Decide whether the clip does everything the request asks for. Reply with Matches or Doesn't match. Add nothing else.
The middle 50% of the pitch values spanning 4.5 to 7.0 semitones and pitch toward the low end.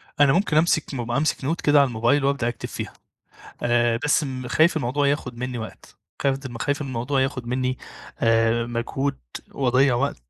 Doesn't match